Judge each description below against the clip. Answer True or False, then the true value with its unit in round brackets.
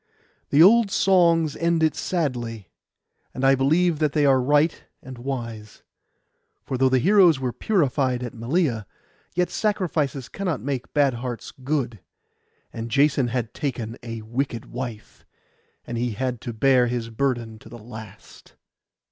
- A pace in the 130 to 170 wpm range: True (145 wpm)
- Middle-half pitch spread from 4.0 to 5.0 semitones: True (4.4 semitones)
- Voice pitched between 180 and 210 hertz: False (130 Hz)